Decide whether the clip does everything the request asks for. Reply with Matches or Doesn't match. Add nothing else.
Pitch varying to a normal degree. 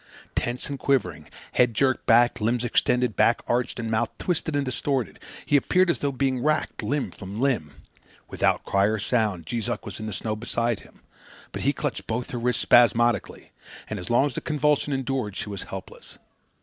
Matches